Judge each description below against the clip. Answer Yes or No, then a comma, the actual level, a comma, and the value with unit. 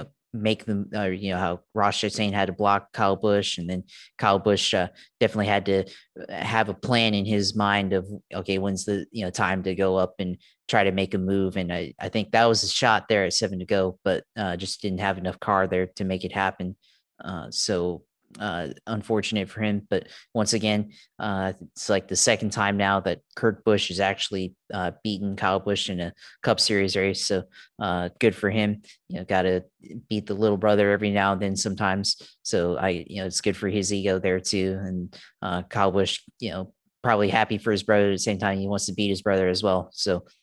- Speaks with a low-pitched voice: Yes, low, 100 Hz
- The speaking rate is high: Yes, fast, 225 wpm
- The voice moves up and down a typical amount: No, narrow, 1.8 semitones